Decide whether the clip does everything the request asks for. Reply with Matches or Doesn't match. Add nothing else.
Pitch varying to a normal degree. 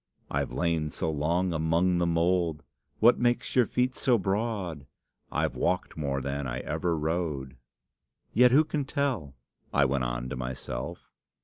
Doesn't match